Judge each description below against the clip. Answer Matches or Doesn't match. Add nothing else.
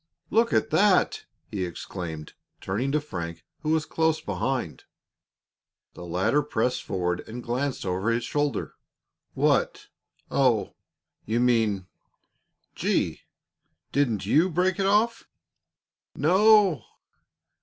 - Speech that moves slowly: Matches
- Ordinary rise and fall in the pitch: Doesn't match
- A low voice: Matches